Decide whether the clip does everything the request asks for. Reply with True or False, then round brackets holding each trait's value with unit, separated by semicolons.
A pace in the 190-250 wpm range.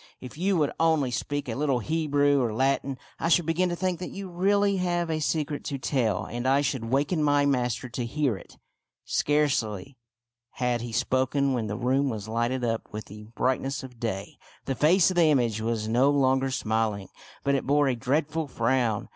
True (195 wpm)